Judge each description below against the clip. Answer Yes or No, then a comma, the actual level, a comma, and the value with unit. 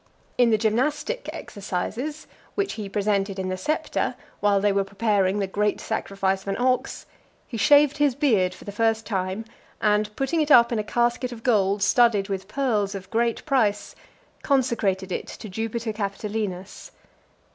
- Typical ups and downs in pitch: Yes, average, 3.5 semitones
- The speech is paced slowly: No, average, 165 wpm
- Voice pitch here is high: Yes, high, 215 Hz